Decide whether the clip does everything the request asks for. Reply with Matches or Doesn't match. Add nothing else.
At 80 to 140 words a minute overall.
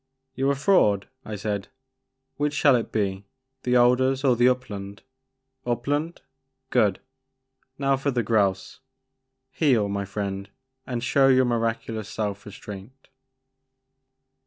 Matches